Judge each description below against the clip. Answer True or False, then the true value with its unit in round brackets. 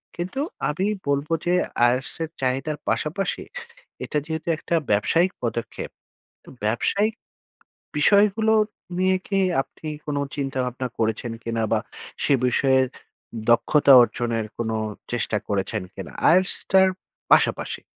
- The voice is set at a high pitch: False (140 Hz)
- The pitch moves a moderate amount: False (7.4 semitones)